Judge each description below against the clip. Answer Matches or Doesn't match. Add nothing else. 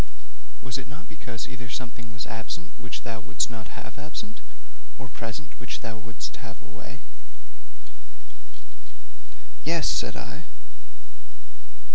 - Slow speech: Matches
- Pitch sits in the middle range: Doesn't match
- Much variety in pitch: Doesn't match